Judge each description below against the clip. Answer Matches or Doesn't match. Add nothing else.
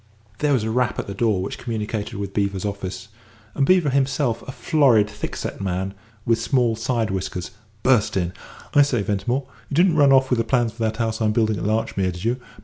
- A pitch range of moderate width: Matches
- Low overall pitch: Matches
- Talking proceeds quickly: Matches